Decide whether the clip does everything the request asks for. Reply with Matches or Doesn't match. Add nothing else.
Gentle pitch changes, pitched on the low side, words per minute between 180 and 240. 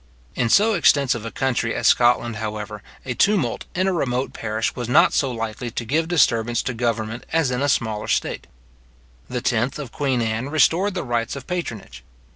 Doesn't match